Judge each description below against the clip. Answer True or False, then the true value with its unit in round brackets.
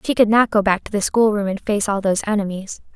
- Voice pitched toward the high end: True (205 Hz)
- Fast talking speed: True (265 wpm)